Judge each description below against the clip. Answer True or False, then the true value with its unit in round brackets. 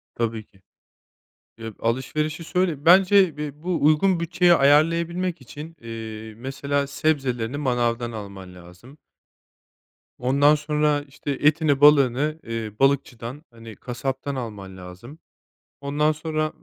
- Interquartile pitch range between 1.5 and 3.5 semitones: False (4.8 semitones)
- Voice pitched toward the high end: False (140 Hz)